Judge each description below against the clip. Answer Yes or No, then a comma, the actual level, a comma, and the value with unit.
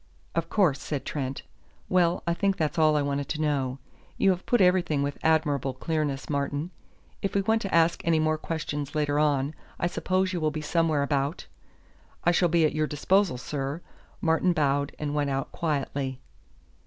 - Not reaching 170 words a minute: No, average, 180 wpm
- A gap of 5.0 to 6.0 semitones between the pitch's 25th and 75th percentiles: No, average, 3.2 semitones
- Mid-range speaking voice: Yes, medium, 155 Hz